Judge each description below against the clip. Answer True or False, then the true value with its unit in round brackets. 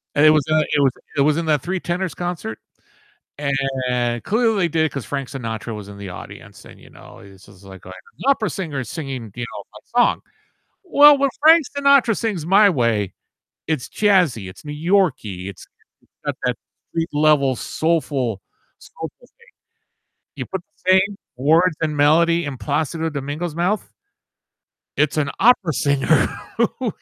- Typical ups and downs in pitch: False (6.0 semitones)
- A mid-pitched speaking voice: True (150 Hz)